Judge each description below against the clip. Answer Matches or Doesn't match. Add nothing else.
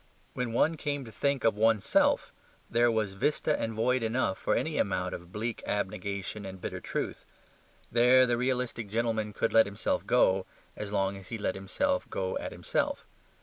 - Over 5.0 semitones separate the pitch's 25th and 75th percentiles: Doesn't match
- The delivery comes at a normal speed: Matches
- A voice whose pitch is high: Doesn't match